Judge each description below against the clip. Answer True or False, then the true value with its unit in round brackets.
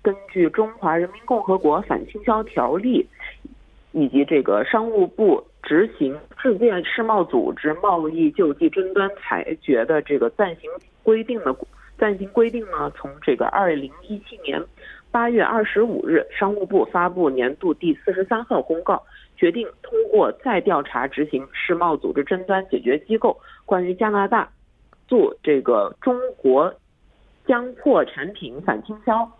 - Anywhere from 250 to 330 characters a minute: False (235 characters per minute)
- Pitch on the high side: True (220 Hz)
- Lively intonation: True (5.8 semitones)